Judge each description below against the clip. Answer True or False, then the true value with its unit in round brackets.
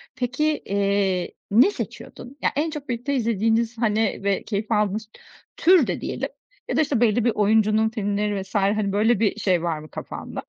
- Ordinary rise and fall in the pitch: True (3.1 semitones)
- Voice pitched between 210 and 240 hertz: True (215 Hz)